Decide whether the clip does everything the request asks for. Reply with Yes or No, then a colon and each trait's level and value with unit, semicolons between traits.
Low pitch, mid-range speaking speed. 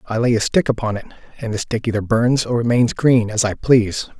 No: low, 115 Hz; fast, 245 wpm